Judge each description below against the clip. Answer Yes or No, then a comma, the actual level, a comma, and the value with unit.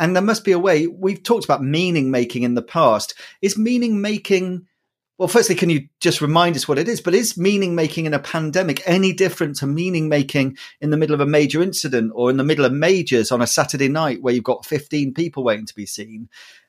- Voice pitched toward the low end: No, medium, 155 Hz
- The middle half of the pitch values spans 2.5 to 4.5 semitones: No, average, 5.1 semitones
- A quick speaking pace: Yes, fast, 235 wpm